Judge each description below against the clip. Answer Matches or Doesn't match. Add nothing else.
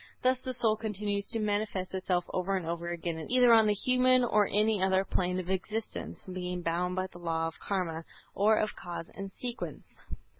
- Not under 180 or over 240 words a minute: Matches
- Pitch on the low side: Doesn't match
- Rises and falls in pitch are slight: Doesn't match